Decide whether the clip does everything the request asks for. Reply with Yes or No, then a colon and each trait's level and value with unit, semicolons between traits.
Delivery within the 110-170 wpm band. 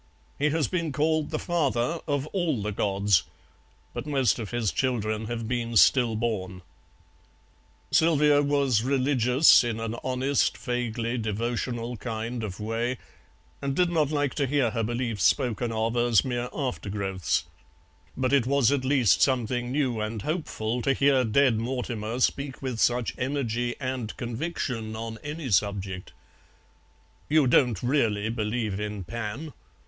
Yes: average, 140 wpm